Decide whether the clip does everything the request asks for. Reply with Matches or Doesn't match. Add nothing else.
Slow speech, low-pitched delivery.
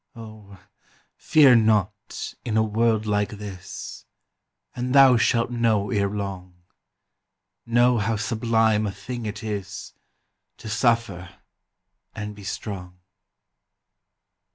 Matches